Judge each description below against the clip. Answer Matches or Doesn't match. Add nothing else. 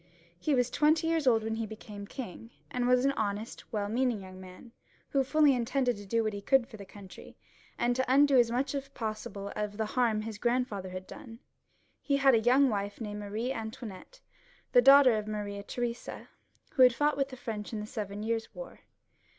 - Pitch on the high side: Matches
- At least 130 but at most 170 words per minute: Doesn't match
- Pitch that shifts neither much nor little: Matches